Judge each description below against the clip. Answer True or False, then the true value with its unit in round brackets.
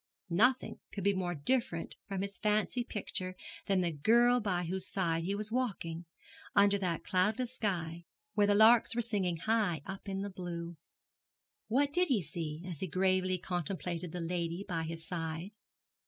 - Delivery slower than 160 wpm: False (170 wpm)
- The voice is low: False (185 Hz)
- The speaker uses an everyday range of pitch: True (3.7 semitones)